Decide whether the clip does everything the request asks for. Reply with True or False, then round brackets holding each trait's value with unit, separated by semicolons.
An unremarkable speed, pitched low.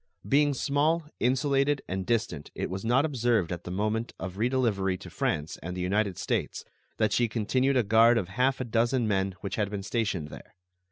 True (190 wpm; 115 Hz)